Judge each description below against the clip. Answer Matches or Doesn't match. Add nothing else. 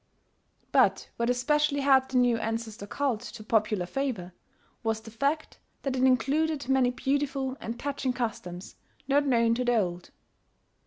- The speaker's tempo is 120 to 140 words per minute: Doesn't match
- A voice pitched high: Matches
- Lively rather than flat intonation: Doesn't match